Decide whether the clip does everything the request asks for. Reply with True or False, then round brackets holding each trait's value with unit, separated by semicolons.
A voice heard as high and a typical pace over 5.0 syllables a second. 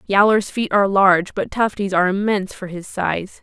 True (195 Hz; 5.5 syllables/s)